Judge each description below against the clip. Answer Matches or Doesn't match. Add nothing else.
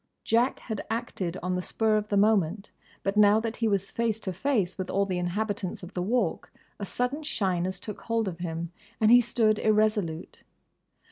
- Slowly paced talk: Doesn't match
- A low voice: Doesn't match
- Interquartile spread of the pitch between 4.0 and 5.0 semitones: Doesn't match